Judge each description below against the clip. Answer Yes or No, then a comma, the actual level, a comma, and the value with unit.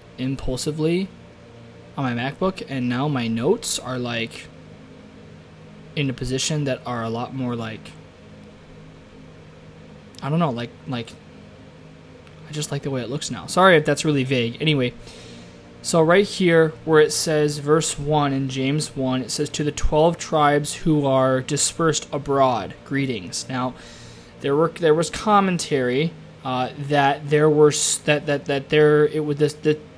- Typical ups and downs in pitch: Yes, average, 3.1 semitones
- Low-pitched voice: No, medium, 145 Hz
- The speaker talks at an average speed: Yes, average, 155 wpm